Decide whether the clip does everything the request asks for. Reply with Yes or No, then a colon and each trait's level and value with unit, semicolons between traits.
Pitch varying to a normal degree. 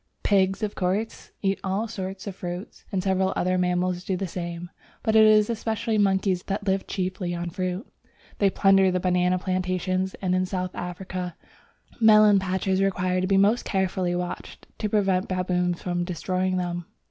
No: narrow, 1.4 semitones